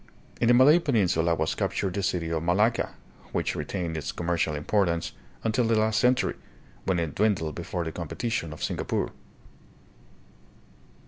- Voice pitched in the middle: No, very low, 90 Hz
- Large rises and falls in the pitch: No, average, 5.0 semitones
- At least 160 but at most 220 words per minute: No, average, 145 wpm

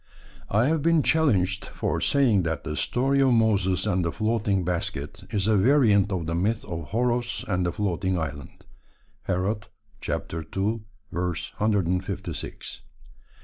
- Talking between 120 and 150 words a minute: Yes, slow, 135 wpm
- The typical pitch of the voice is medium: No, low, 100 Hz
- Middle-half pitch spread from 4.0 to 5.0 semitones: Yes, average, 4.4 semitones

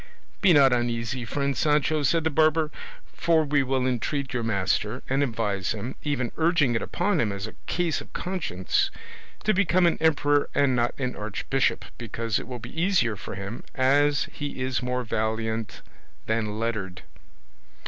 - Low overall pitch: Yes, low, 130 Hz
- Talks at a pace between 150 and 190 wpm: Yes, average, 165 wpm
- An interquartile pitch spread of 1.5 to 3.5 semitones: No, average, 4.8 semitones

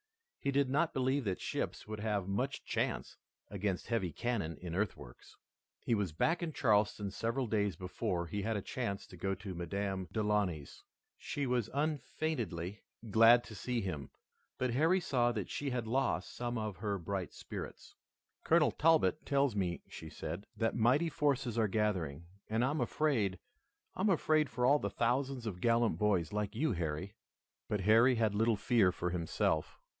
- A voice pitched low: Yes, low, 110 Hz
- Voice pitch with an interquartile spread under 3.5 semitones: No, average, 5.0 semitones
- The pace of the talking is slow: No, average, 170 wpm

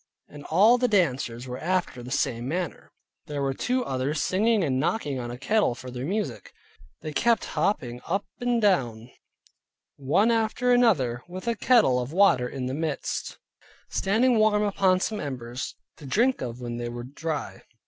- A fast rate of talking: No, average, 170 wpm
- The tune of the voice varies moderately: No, wide, 8.7 semitones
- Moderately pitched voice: Yes, medium, 155 Hz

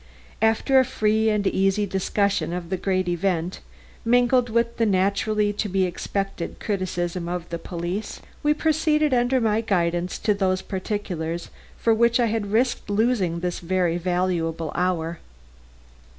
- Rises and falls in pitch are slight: No, average, 4.0 semitones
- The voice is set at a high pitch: Yes, high, 195 Hz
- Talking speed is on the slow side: No, average, 145 wpm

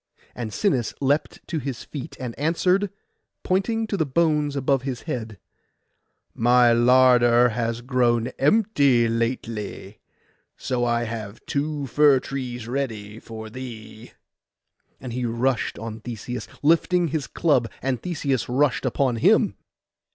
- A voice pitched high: No, low, 125 Hz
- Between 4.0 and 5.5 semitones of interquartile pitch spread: No, average, 3.6 semitones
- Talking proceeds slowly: Yes, slow, 130 wpm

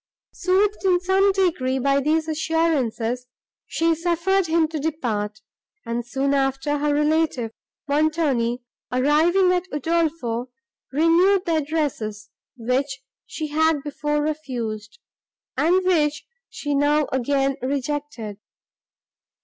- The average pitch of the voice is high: Yes, very high, 295 Hz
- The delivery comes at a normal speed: No, slow, 110 wpm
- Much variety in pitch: No, average, 4.1 semitones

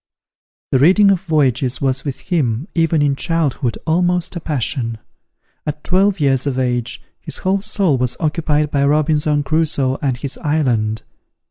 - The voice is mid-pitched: Yes, medium, 150 Hz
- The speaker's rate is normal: Yes, average, 150 wpm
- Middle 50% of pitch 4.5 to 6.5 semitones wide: No, average, 4.0 semitones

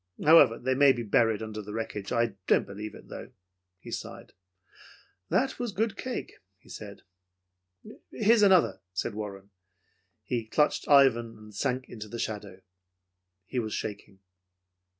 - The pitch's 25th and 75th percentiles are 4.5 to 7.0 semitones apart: Yes, average, 4.9 semitones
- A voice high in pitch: No, low, 115 Hz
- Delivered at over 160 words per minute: No, average, 145 wpm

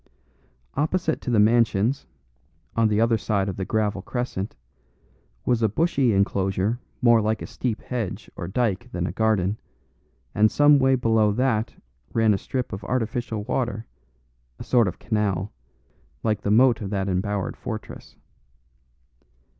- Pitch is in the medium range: No, low, 110 Hz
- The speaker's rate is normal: Yes, average, 145 wpm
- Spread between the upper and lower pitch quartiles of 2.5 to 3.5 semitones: Yes, average, 3.2 semitones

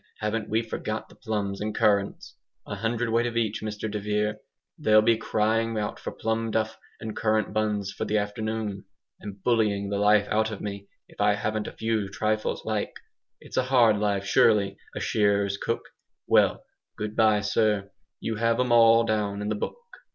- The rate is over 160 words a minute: Yes, average, 180 wpm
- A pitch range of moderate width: No, narrow, 1.4 semitones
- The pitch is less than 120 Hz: Yes, low, 110 Hz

